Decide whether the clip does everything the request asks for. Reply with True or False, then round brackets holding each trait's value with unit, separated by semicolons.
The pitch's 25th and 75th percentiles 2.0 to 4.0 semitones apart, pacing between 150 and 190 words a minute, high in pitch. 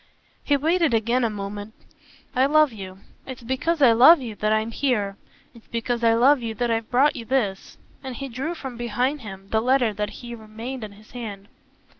False (3.5 semitones; 200 wpm; 235 Hz)